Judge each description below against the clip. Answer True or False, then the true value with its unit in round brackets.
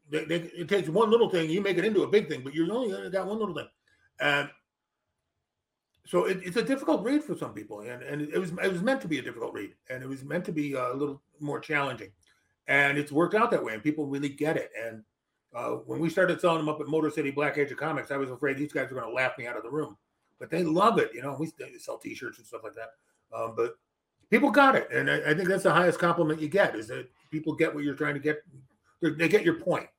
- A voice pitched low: False (160 Hz)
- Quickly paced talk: True (270 wpm)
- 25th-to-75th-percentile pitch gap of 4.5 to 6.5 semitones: True (4.8 semitones)